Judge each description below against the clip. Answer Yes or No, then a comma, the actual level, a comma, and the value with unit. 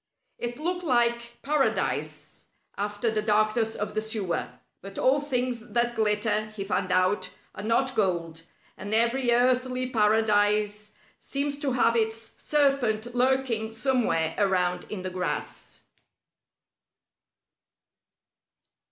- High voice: Yes, high, 220 Hz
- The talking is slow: Yes, slow, 115 wpm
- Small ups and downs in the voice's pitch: No, average, 3.3 semitones